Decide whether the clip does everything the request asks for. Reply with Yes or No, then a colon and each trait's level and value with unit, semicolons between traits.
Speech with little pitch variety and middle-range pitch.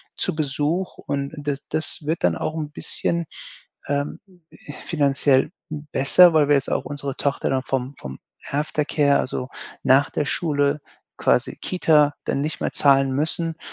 Yes: narrow, 2.1 semitones; medium, 145 Hz